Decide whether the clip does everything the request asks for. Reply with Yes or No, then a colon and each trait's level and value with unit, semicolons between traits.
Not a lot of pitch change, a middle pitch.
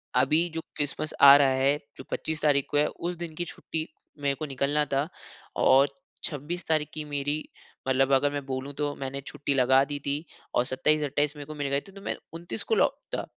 Yes: narrow, 1.9 semitones; medium, 145 Hz